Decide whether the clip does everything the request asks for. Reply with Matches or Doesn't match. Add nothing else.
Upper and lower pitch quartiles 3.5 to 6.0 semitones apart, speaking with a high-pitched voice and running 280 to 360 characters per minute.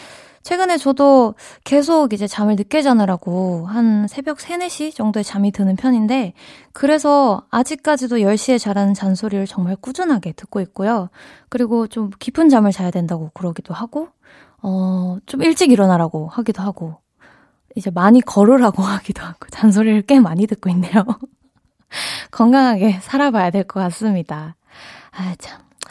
Matches